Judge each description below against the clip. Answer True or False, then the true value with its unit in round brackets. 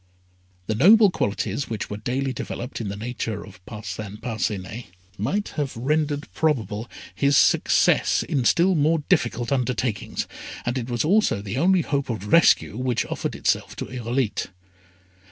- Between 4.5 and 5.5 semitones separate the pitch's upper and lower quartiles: True (5.0 semitones)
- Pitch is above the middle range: False (125 Hz)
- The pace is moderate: True (150 wpm)